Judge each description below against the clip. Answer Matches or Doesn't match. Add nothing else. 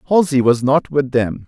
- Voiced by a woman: Doesn't match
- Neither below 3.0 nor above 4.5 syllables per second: Doesn't match